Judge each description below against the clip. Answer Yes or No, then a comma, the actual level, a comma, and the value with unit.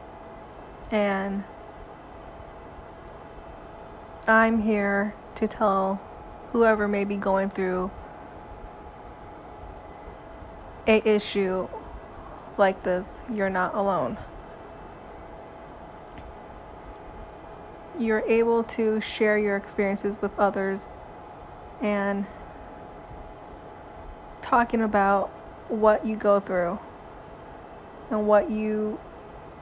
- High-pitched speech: Yes, high, 205 Hz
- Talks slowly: Yes, slow, 70 wpm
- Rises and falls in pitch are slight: Yes, narrow, 1.9 semitones